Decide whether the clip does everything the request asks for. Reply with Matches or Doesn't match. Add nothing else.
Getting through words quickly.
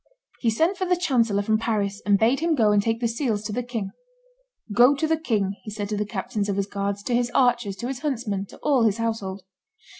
Matches